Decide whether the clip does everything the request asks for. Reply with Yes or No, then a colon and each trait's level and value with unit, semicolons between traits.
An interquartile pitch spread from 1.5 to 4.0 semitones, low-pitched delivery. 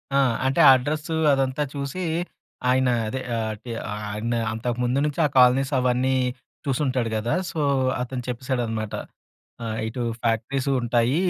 Yes: narrow, 2.6 semitones; low, 125 Hz